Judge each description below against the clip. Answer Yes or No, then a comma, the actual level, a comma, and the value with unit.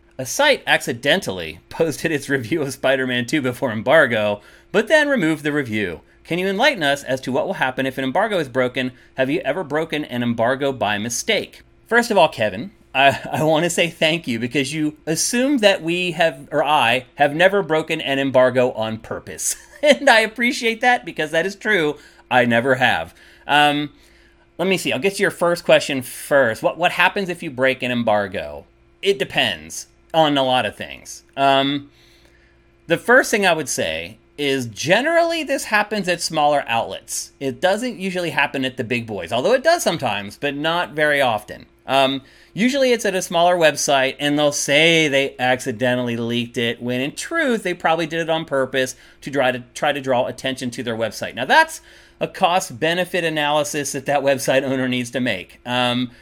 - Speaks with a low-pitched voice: No, medium, 145 Hz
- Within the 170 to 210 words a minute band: Yes, average, 190 wpm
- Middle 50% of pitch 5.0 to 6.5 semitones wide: Yes, wide, 5.4 semitones